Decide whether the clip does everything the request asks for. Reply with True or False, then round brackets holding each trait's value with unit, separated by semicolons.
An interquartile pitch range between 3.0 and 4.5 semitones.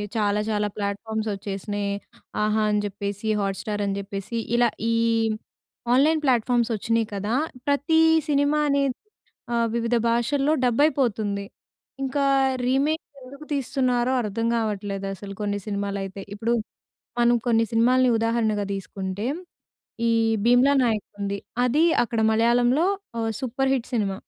True (3.7 semitones)